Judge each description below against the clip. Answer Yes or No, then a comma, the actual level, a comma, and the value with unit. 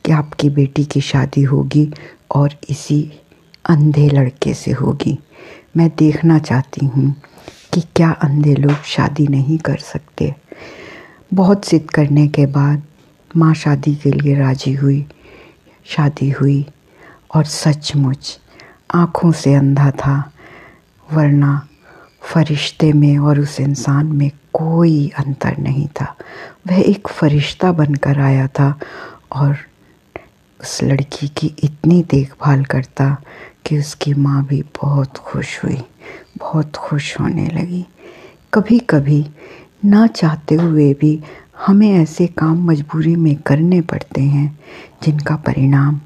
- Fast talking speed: No, average, 120 wpm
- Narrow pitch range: Yes, narrow, 2.1 semitones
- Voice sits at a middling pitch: Yes, medium, 150 Hz